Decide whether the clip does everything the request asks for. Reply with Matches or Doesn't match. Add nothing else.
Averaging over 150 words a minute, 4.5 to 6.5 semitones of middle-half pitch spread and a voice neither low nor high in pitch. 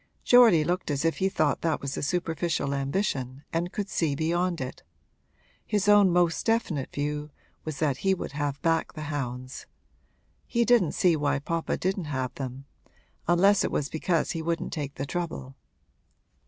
Doesn't match